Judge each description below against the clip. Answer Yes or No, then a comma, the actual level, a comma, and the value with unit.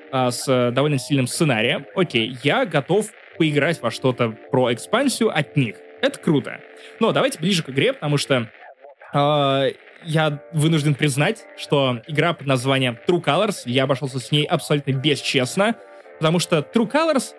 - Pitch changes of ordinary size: Yes, average, 3.7 semitones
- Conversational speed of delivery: Yes, average, 150 wpm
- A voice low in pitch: No, medium, 145 Hz